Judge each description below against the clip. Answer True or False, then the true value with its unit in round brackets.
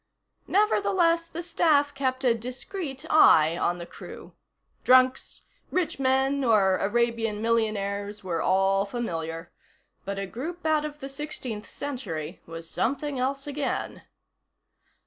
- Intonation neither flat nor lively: False (6.5 semitones)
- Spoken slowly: True (125 wpm)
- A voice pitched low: False (250 Hz)